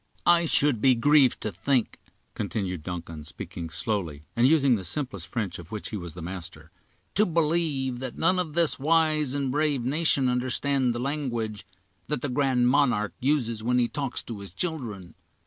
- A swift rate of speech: No, average, 175 wpm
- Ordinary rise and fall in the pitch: No, wide, 6.0 semitones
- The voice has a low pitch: Yes, low, 125 Hz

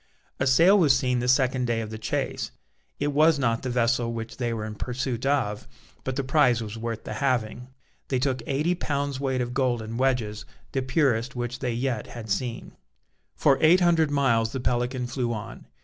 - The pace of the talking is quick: No, average, 195 wpm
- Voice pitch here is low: Yes, low, 125 Hz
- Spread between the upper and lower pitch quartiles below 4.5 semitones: Yes, average, 2.8 semitones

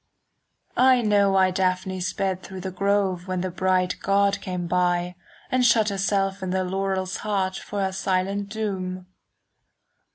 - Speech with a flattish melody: Yes, narrow, 1.4 semitones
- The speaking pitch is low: No, high, 190 Hz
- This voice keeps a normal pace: Yes, average, 155 wpm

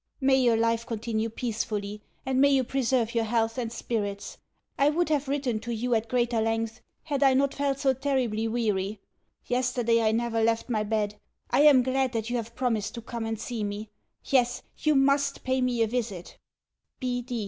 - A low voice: No, high, 235 Hz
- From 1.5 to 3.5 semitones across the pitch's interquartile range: Yes, average, 2.8 semitones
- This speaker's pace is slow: No, average, 185 wpm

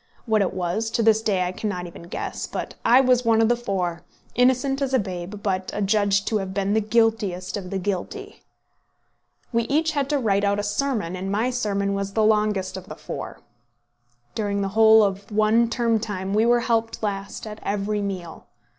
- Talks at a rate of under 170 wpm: No, average, 200 wpm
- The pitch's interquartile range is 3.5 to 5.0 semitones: No, average, 2.8 semitones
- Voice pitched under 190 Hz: No, high, 210 Hz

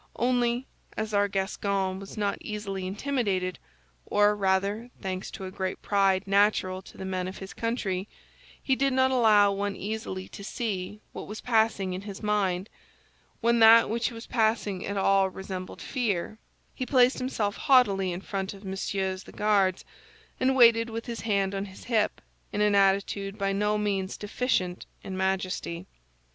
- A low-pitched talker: No, high, 200 Hz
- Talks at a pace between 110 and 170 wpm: Yes, average, 160 wpm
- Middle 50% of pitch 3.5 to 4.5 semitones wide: No, average, 2.7 semitones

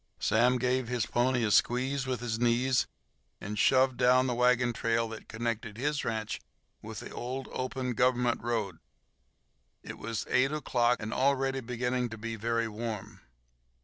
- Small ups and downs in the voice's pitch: Yes, narrow, 1.9 semitones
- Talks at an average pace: Yes, average, 155 wpm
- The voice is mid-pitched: No, low, 120 Hz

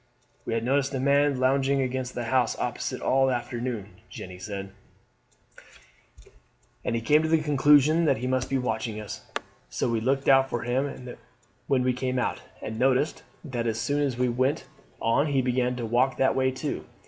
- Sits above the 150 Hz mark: No, low, 130 Hz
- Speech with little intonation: Yes, narrow, 2.2 semitones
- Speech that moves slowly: No, average, 185 wpm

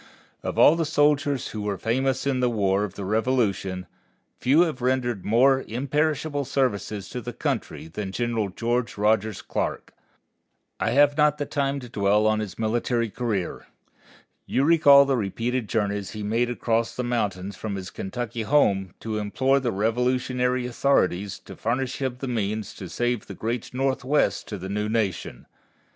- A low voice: Yes, low, 120 Hz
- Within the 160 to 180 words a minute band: Yes, average, 165 wpm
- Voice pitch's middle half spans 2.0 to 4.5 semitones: Yes, average, 4.1 semitones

